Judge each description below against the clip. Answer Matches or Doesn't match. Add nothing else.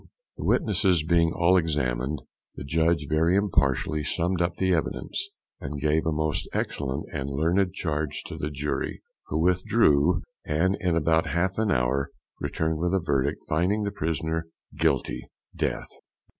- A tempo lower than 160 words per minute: Matches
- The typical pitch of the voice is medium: Doesn't match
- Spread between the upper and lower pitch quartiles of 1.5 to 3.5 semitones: Matches